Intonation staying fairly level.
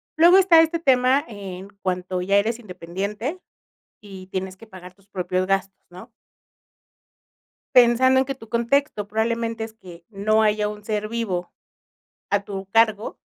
No: average, 3.7 semitones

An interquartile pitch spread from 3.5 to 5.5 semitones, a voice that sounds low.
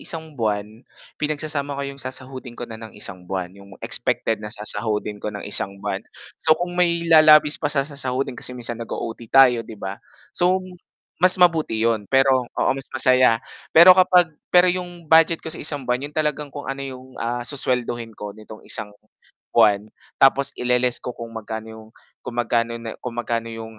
Yes: average, 5.1 semitones; low, 125 Hz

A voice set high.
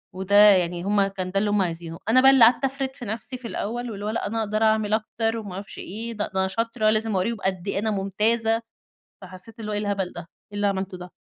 Yes: high, 210 Hz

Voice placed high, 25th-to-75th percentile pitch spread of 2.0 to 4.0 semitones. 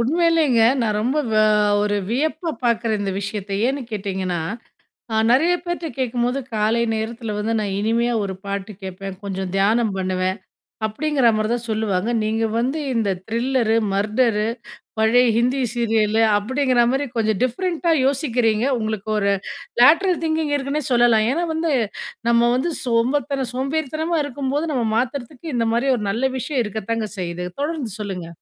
No: high, 235 Hz; average, 4.4 semitones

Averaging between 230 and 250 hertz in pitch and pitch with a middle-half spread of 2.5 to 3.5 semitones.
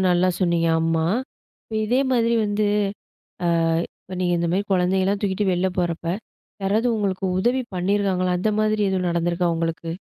No: medium, 185 Hz; average, 2.9 semitones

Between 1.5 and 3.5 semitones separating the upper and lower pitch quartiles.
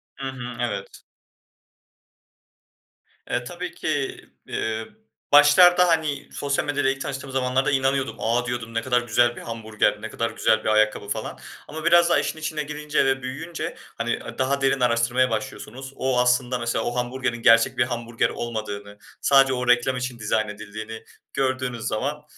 Yes: average, 2.9 semitones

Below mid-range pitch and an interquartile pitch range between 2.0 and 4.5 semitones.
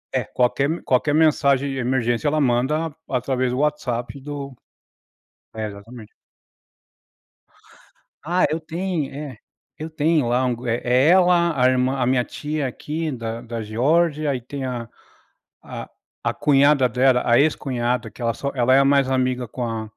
Yes: low, 130 Hz; average, 3.4 semitones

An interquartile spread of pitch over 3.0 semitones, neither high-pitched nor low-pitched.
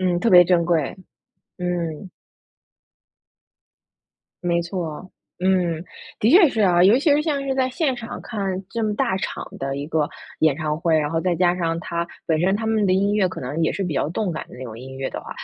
Yes: average, 4.4 semitones; medium, 180 Hz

